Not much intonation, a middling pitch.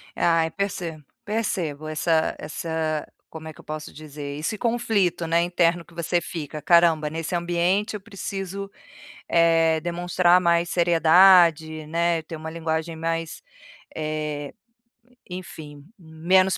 Yes: narrow, 2.0 semitones; medium, 165 Hz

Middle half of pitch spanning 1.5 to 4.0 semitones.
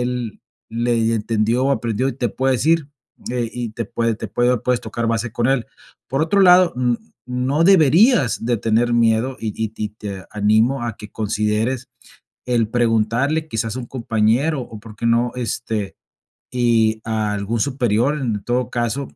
Yes: narrow, 2.4 semitones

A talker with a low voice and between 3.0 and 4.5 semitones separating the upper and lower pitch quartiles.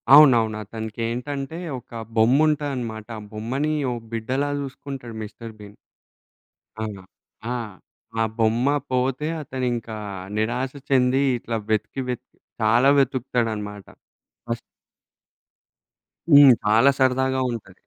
Yes: low, 125 Hz; average, 3.3 semitones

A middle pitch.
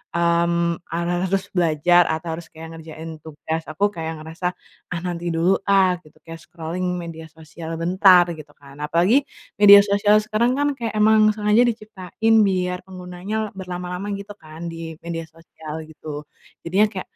Yes: medium, 175 Hz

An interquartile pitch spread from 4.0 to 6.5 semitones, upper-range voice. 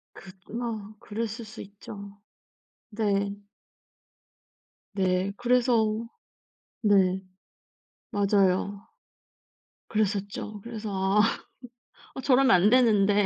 No: narrow, 2.2 semitones; high, 205 Hz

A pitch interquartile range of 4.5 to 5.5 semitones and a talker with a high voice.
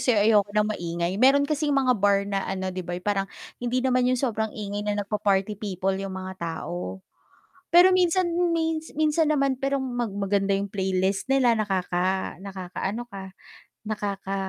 Yes: average, 5.0 semitones; high, 205 Hz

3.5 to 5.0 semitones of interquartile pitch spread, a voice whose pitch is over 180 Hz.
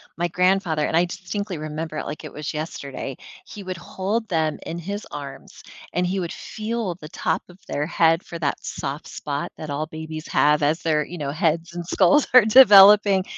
No: average, 3.8 semitones; medium, 170 Hz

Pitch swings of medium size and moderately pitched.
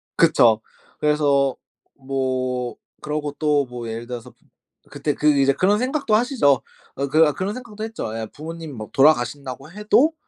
Yes: average, 4.7 semitones; medium, 145 Hz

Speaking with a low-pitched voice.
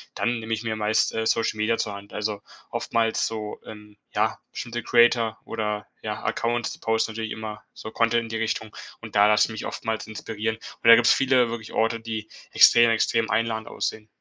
Yes: low, 110 Hz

